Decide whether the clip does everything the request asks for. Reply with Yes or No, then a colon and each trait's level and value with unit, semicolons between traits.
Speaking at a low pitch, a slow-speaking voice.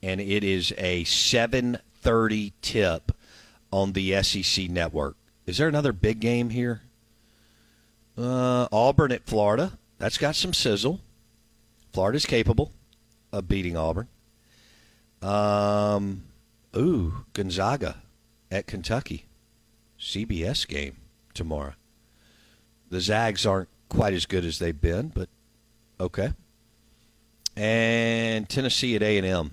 Yes: low, 110 Hz; slow, 105 wpm